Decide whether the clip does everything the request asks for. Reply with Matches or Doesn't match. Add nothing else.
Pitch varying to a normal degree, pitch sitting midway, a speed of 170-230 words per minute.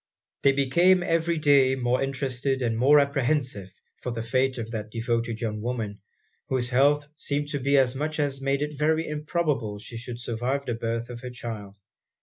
Doesn't match